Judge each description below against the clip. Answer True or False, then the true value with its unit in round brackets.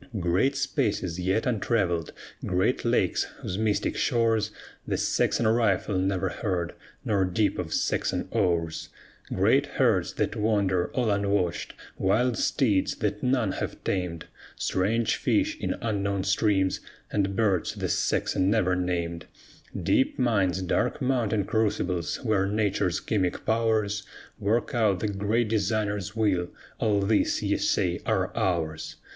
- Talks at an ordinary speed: False (130 wpm)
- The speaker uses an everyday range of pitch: True (3.1 semitones)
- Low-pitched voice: True (100 Hz)